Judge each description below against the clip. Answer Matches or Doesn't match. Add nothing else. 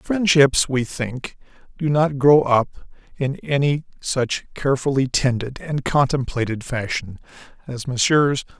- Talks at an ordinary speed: Doesn't match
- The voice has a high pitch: Doesn't match